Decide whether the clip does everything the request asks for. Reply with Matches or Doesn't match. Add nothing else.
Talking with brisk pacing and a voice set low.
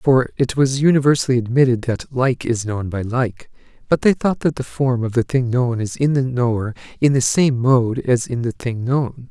Matches